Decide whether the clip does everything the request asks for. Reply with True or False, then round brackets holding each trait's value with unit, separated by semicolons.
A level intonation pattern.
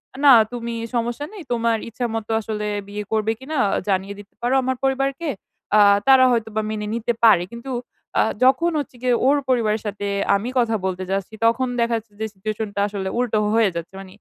False (3.1 semitones)